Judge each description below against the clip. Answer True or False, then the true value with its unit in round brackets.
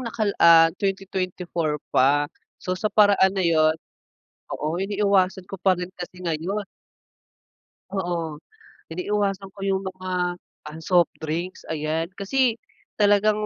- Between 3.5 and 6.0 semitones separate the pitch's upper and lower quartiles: False (2.9 semitones)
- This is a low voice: False (185 Hz)